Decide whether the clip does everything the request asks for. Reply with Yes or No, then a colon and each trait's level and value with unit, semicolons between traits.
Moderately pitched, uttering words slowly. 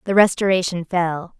Yes: medium, 180 Hz; slow, 130 wpm